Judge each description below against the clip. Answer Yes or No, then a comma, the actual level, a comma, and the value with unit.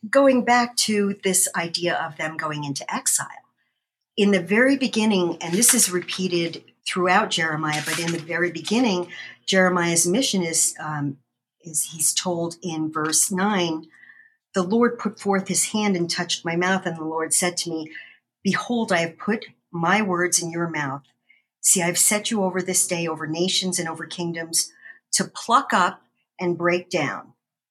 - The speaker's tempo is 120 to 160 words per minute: No, average, 170 wpm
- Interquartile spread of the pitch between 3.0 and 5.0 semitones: Yes, average, 3.6 semitones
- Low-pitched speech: No, medium, 180 Hz